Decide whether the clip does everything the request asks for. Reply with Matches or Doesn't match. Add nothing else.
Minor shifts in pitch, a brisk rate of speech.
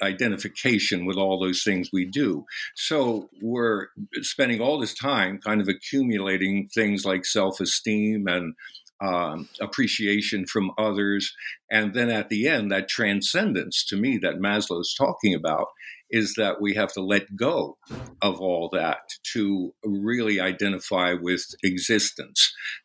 Doesn't match